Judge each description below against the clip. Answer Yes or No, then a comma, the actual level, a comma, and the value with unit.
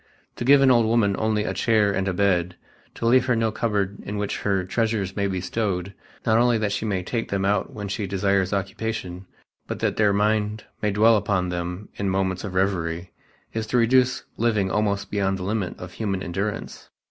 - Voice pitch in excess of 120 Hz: No, low, 100 Hz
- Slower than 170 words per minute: No, fast, 205 wpm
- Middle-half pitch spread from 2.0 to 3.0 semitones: Yes, narrow, 2.6 semitones